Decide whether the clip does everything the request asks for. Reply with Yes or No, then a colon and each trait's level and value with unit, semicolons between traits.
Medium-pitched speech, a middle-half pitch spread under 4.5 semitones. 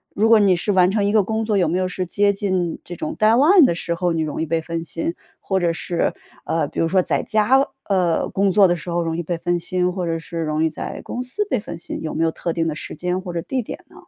Yes: medium, 180 Hz; average, 3.6 semitones